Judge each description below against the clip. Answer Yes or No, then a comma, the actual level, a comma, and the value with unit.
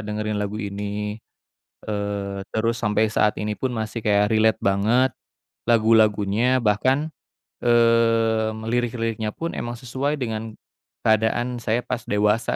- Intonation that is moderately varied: No, narrow, 2.1 semitones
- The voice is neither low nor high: No, low, 110 Hz